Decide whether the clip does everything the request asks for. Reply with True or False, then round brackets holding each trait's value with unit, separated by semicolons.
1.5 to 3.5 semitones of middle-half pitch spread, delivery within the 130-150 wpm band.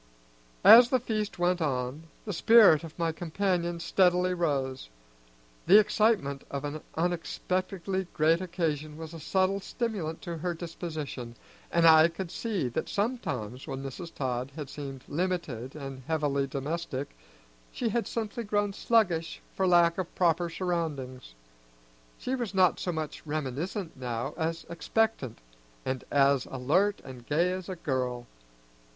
False (5.1 semitones; 140 wpm)